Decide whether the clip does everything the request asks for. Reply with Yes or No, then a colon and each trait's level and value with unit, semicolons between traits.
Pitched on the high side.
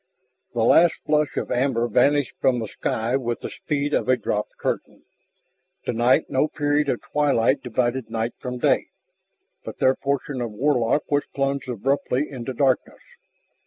No: low, 130 Hz